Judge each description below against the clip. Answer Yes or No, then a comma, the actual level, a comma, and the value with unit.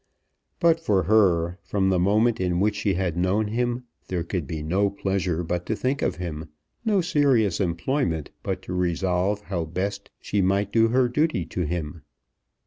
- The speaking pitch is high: No, very low, 95 Hz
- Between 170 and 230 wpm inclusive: Yes, average, 175 wpm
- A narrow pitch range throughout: No, average, 4.0 semitones